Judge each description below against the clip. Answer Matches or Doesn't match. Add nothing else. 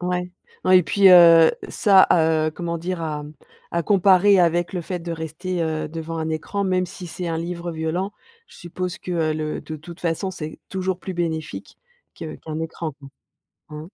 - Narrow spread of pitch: Matches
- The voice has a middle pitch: Matches